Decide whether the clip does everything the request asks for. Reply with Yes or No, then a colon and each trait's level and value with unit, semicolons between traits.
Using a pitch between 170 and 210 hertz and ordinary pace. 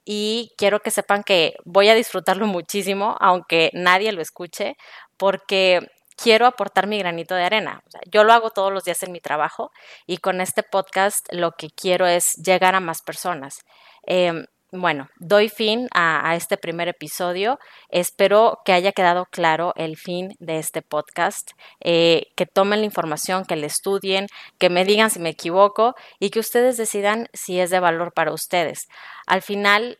Yes: medium, 185 Hz; average, 175 wpm